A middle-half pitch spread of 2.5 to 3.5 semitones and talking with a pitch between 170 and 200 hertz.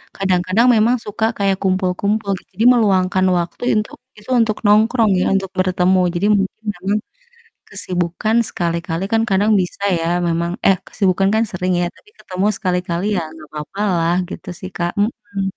Yes: average, 2.8 semitones; high, 190 Hz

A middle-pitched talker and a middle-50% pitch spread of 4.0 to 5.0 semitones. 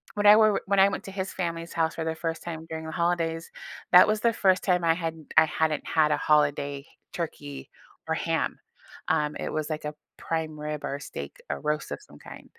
No: medium, 160 Hz; average, 2.8 semitones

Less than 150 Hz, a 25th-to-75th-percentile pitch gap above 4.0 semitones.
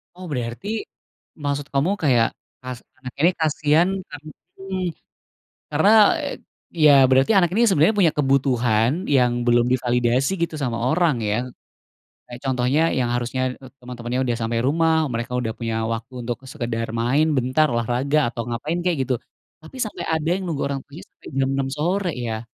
Yes: low, 135 Hz; average, 4.5 semitones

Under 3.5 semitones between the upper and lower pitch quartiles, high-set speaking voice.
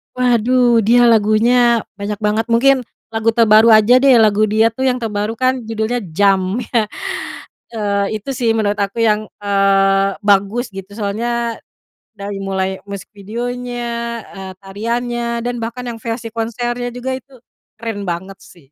Yes: average, 3.0 semitones; high, 225 Hz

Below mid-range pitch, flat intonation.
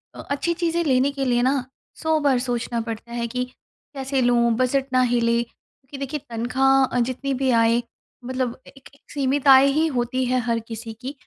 No: very high, 255 Hz; narrow, 2.3 semitones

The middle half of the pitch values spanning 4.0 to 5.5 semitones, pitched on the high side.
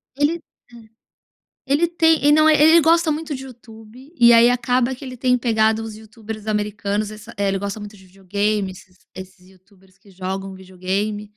Yes: average, 4.7 semitones; high, 220 Hz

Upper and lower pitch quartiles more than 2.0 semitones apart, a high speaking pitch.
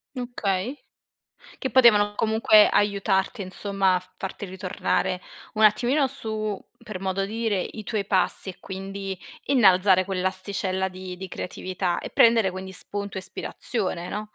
Yes: narrow, 2.4 semitones; high, 195 Hz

